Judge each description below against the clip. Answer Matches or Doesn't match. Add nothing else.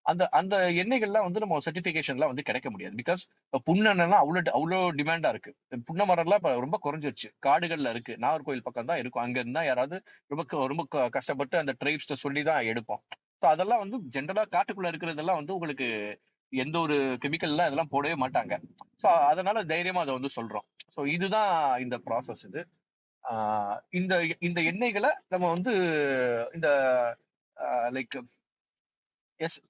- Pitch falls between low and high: Matches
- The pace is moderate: Doesn't match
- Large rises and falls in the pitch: Matches